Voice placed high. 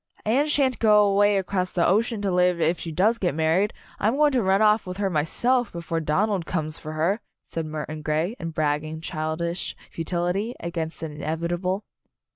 No: medium, 180 Hz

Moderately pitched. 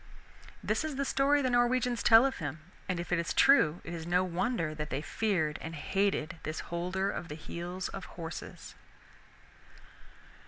Yes: medium, 180 Hz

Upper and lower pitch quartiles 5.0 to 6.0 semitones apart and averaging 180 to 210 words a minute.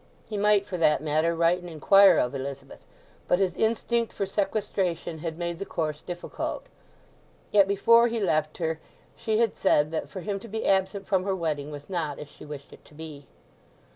No: average, 4.5 semitones; average, 195 wpm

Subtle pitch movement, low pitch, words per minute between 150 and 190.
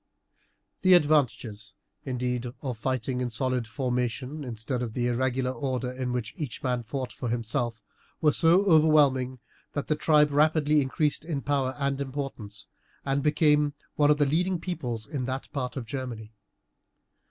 No: average, 3.2 semitones; low, 130 Hz; average, 155 wpm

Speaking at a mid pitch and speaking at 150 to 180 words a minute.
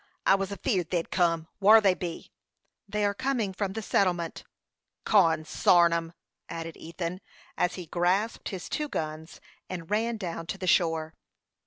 Yes: medium, 180 Hz; average, 155 wpm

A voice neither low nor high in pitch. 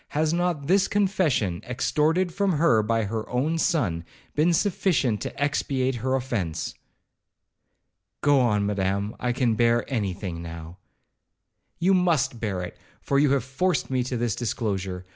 No: low, 125 Hz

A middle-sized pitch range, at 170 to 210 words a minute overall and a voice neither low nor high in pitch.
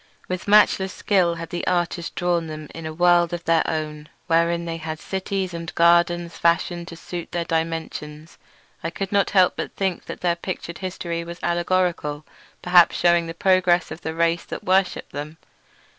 No: narrow, 1.3 semitones; average, 175 wpm; medium, 170 Hz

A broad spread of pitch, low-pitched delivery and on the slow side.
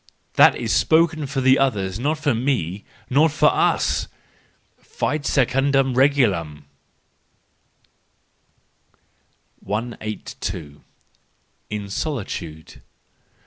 Yes: wide, 6.1 semitones; low, 130 Hz; slow, 80 wpm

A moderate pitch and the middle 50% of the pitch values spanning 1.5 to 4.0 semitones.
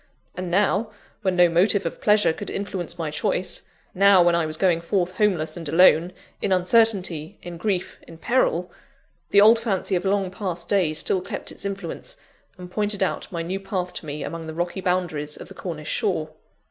Yes: medium, 180 Hz; average, 2.9 semitones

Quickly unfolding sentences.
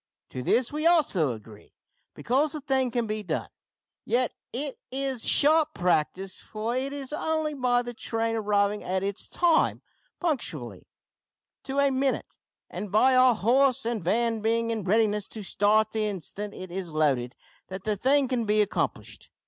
No: average, 165 wpm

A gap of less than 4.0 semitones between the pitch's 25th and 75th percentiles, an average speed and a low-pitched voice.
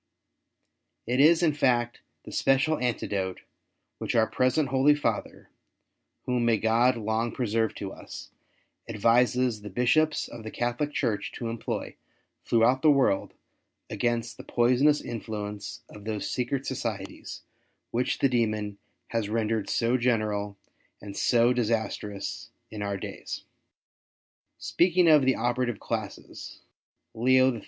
No: average, 3.0 semitones; slow, 130 wpm; low, 120 Hz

